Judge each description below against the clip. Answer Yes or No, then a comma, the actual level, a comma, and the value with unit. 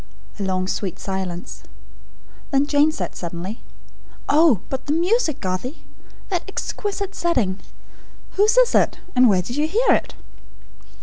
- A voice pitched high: Yes, very high, 275 Hz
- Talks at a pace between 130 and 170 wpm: Yes, average, 140 wpm